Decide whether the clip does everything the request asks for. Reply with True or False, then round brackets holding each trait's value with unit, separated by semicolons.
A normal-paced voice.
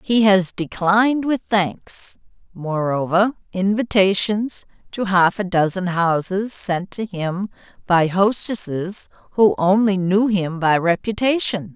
False (115 wpm)